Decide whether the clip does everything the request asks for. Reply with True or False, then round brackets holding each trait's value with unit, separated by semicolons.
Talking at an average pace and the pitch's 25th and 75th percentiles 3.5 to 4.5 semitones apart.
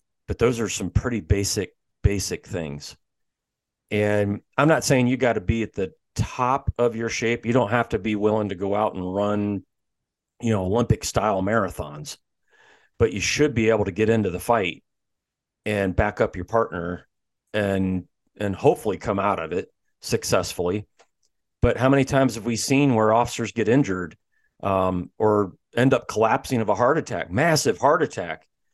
False (175 wpm; 2.9 semitones)